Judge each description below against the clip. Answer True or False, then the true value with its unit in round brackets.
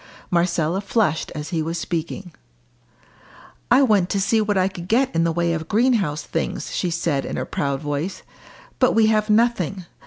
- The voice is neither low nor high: True (180 Hz)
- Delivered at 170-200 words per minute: True (185 wpm)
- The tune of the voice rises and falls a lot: False (4.5 semitones)